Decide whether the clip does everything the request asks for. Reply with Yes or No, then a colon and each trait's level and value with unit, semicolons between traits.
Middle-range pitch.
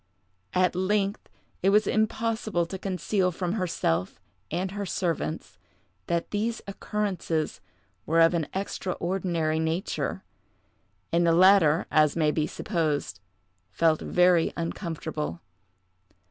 Yes: medium, 175 Hz